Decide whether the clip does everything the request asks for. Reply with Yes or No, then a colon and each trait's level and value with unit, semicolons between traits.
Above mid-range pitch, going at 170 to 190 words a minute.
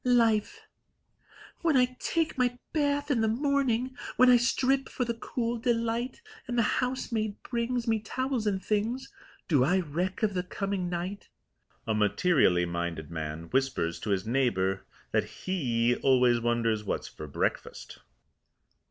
No: high, 210 Hz; average, 145 wpm